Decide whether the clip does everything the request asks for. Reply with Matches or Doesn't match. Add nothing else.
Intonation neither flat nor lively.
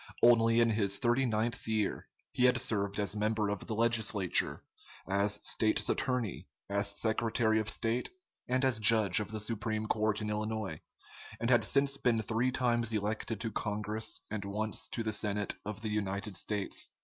Doesn't match